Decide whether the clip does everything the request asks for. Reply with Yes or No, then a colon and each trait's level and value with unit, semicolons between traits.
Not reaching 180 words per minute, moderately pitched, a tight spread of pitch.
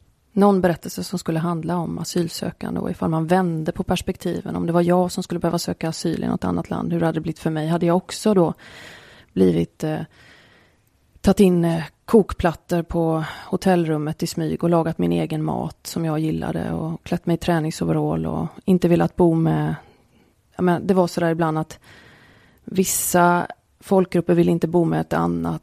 No: average, 185 wpm; medium, 170 Hz; narrow, 2.3 semitones